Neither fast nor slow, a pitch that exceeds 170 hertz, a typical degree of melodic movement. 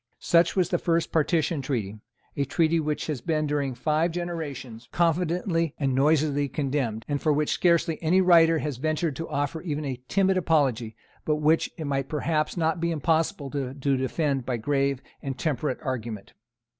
No: average, 170 wpm; medium, 150 Hz; average, 3.3 semitones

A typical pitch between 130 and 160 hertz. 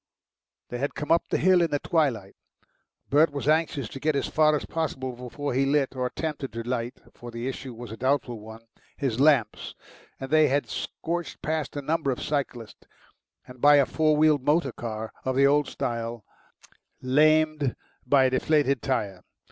Yes: medium, 140 Hz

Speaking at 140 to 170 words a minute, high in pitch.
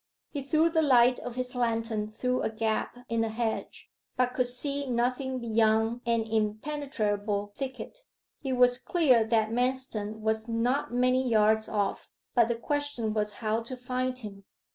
Yes: average, 160 wpm; high, 235 Hz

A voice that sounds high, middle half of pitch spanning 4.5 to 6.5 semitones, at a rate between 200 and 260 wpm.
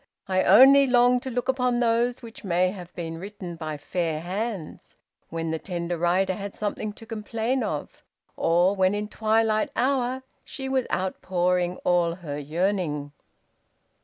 No: high, 195 Hz; average, 5.0 semitones; average, 150 wpm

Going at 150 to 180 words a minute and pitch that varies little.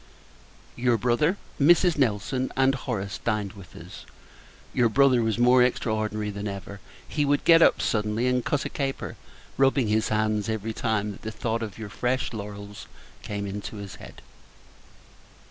No: average, 160 wpm; average, 3.7 semitones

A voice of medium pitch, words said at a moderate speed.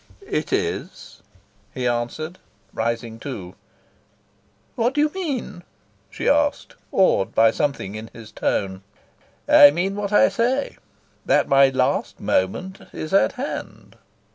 No: medium, 150 Hz; slow, 125 wpm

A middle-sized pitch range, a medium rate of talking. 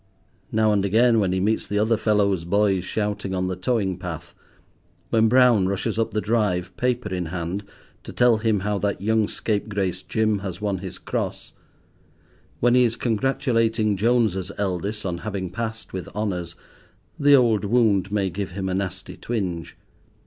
Yes: average, 3.1 semitones; average, 165 wpm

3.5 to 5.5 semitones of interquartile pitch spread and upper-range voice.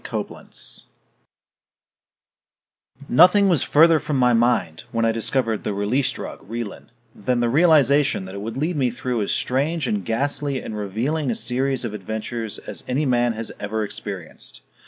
No: average, 4.3 semitones; low, 120 Hz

